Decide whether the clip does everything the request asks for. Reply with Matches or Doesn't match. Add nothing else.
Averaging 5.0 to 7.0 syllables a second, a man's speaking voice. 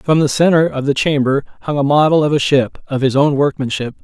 Matches